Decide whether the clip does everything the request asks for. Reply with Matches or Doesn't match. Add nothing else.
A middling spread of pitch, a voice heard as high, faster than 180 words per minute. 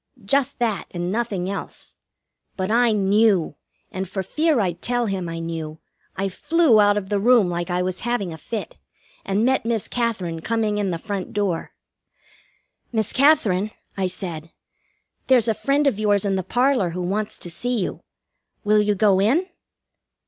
Doesn't match